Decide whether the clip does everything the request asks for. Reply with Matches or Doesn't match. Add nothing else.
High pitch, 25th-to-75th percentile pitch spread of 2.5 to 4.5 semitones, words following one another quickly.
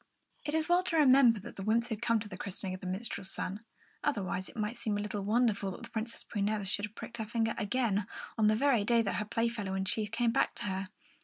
Matches